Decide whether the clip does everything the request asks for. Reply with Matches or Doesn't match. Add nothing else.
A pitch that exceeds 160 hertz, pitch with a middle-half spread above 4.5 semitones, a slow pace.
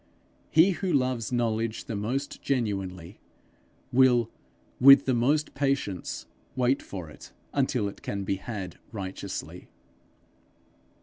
Doesn't match